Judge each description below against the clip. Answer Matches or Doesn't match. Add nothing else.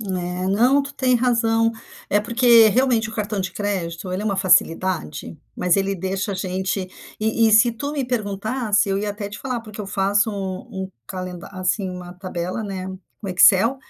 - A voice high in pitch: Matches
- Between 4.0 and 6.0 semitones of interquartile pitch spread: Doesn't match